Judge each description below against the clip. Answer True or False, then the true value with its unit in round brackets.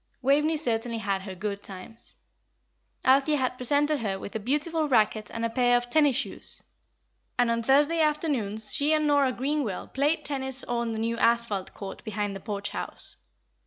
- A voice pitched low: False (245 Hz)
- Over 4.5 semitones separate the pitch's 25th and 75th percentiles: True (5.0 semitones)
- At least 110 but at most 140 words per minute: False (170 wpm)